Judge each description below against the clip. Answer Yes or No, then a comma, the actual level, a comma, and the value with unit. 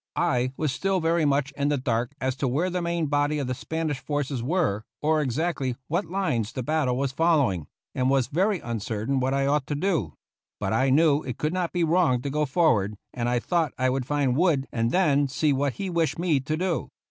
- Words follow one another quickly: Yes, fast, 225 wpm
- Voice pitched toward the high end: No, medium, 145 Hz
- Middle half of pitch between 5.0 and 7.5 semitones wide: No, average, 4.2 semitones